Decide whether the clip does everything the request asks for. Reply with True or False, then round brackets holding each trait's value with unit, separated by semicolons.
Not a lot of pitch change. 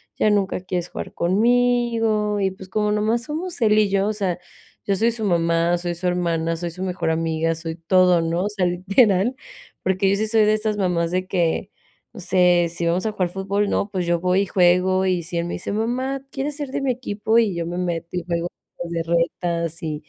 False (3.7 semitones)